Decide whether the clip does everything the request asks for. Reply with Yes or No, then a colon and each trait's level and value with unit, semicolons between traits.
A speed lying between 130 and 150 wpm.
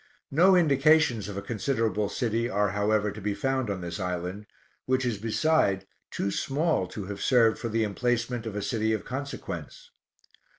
No: average, 170 wpm